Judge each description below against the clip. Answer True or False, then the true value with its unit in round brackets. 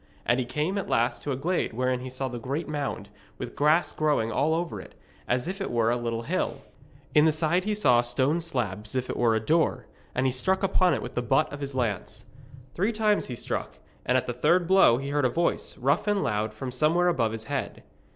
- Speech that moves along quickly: True (240 wpm)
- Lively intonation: True (5.8 semitones)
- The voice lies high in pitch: False (135 Hz)